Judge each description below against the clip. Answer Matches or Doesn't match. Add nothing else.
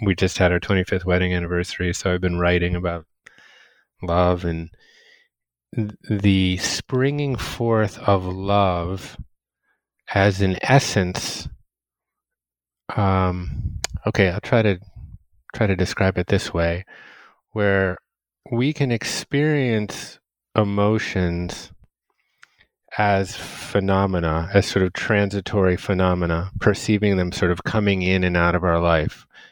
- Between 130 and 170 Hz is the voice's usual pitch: Doesn't match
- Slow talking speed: Matches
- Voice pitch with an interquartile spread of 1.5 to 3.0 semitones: Matches